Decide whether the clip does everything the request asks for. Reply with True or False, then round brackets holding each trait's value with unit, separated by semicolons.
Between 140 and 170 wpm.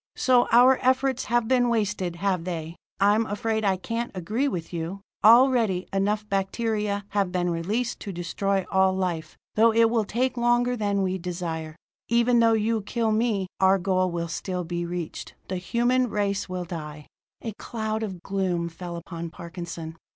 True (165 wpm)